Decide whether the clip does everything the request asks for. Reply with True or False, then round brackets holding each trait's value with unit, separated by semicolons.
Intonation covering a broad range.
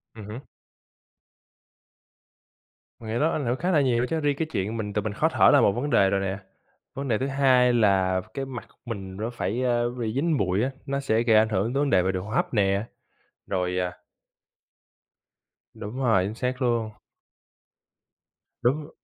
False (5.0 semitones)